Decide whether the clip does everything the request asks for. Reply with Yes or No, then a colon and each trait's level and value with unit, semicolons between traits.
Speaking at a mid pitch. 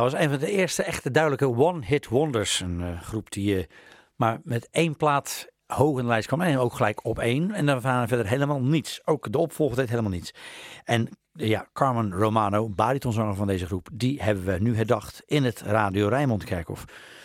No: low, 120 Hz